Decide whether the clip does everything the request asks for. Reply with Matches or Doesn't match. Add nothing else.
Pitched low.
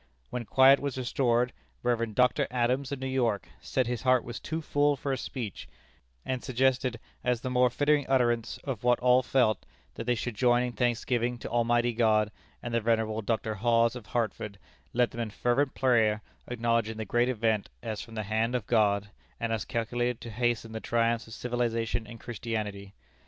Matches